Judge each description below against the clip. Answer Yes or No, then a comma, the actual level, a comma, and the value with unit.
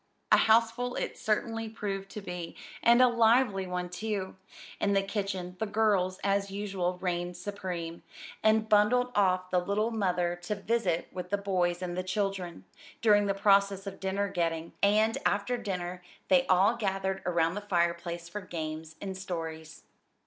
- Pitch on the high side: Yes, high, 195 Hz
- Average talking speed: Yes, average, 160 wpm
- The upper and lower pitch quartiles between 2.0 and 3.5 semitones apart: Yes, average, 2.8 semitones